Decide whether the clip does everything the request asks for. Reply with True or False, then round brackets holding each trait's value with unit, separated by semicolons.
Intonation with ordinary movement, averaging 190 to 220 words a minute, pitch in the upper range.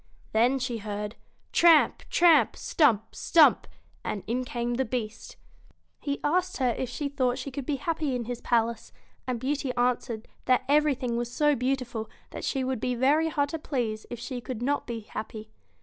False (3.4 semitones; 180 wpm; 250 Hz)